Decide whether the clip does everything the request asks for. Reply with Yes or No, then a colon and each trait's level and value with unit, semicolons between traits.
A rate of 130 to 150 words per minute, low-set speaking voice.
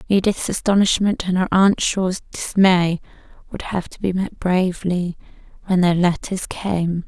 No: average, 145 wpm; medium, 185 Hz